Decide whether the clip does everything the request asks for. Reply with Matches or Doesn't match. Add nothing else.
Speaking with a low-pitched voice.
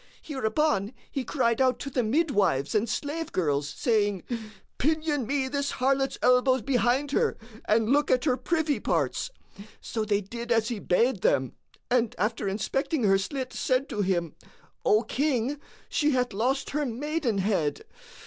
Doesn't match